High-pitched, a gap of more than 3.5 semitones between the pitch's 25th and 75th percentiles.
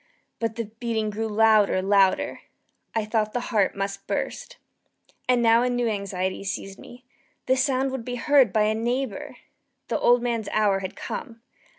No: high, 225 Hz; average, 3.2 semitones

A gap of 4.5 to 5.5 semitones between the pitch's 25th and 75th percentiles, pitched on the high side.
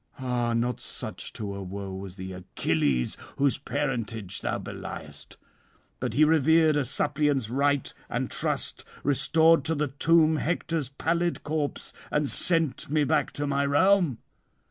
No: average, 5.1 semitones; medium, 140 Hz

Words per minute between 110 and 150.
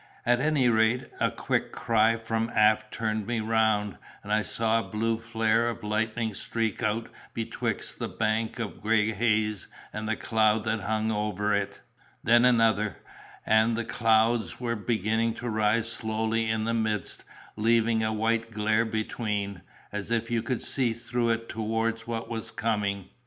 No: average, 160 wpm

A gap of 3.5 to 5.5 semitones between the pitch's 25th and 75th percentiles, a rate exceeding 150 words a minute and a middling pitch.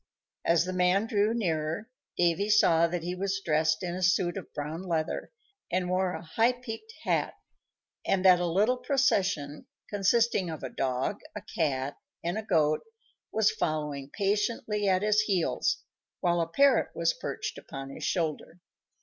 Yes: average, 4.5 semitones; average, 160 wpm; medium, 180 Hz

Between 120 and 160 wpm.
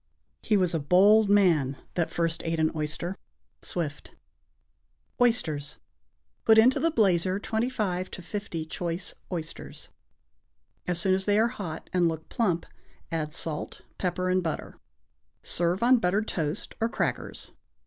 Yes: average, 140 wpm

